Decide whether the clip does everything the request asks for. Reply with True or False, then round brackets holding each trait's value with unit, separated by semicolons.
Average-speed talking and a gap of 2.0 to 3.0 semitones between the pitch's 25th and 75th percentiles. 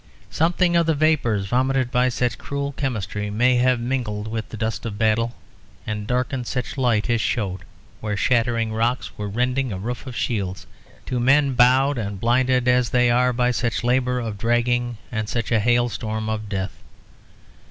True (175 wpm; 2.5 semitones)